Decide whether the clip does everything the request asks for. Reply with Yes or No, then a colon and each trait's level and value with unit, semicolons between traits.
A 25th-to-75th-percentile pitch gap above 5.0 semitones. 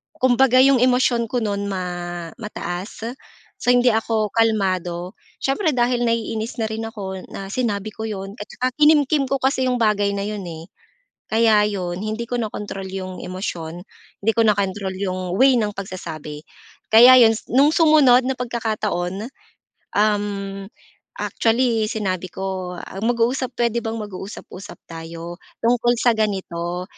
No: average, 4.0 semitones